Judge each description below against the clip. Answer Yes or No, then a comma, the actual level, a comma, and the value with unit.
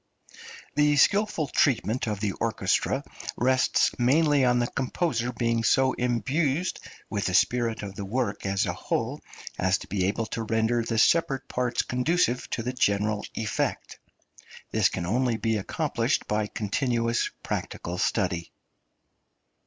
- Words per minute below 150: Yes, average, 140 wpm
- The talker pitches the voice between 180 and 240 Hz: No, low, 120 Hz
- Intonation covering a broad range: No, average, 3.6 semitones